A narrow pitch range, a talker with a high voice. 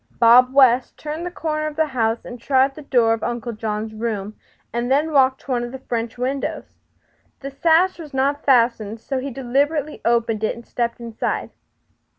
No: average, 3.4 semitones; very high, 255 Hz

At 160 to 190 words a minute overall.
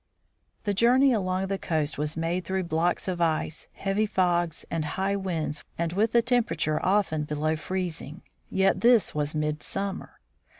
No: average, 145 wpm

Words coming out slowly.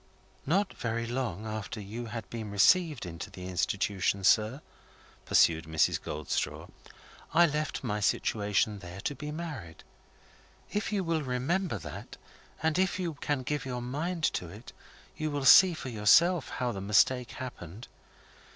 No: average, 150 wpm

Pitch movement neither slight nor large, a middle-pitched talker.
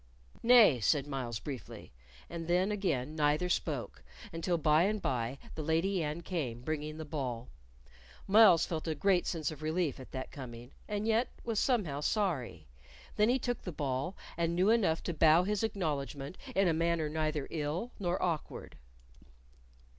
Yes: average, 4.5 semitones; medium, 160 Hz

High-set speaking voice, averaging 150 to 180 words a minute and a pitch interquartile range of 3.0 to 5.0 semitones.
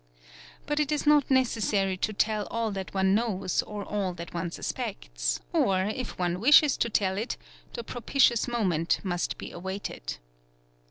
Yes: high, 200 Hz; average, 160 wpm; average, 4.4 semitones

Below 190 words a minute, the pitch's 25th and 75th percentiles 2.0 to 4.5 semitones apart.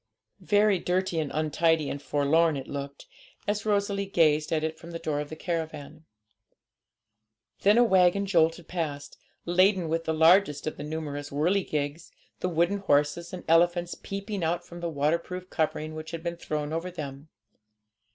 Yes: average, 160 wpm; average, 3.1 semitones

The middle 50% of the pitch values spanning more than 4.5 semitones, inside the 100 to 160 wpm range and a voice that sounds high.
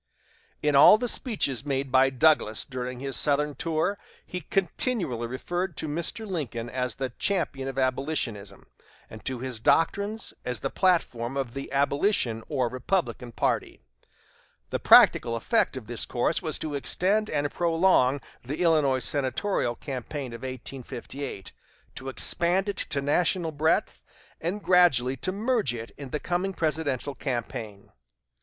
No: wide, 5.4 semitones; average, 145 wpm; medium, 140 Hz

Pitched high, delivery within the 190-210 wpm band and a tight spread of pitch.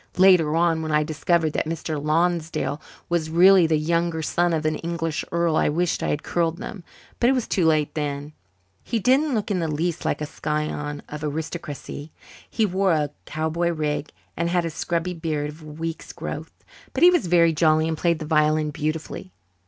No: medium, 160 Hz; average, 195 wpm; narrow, 2.1 semitones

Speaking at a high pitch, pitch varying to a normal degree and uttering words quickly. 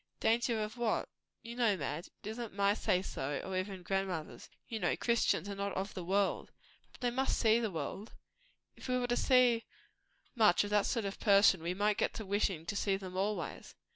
Yes: high, 205 Hz; average, 3.2 semitones; fast, 210 wpm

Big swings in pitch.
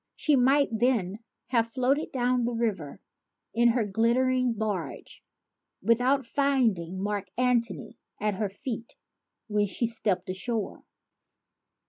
No: average, 3.5 semitones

